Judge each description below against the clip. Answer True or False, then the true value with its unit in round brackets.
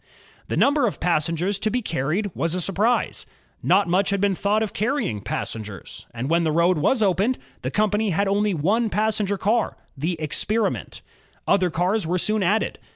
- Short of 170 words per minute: False (180 wpm)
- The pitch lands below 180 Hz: False (195 Hz)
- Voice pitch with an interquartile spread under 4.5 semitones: True (4.1 semitones)